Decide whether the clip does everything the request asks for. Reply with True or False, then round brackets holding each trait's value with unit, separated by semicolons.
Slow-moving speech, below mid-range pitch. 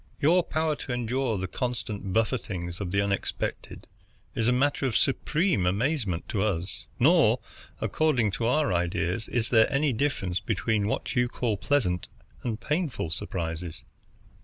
False (145 wpm; 110 Hz)